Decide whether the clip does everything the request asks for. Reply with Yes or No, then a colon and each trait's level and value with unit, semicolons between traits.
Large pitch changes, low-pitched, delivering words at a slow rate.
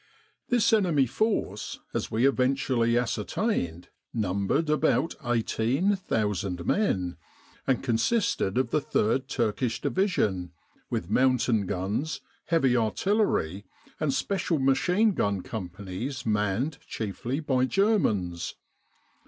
Yes: wide, 7.3 semitones; low, 125 Hz; slow, 100 wpm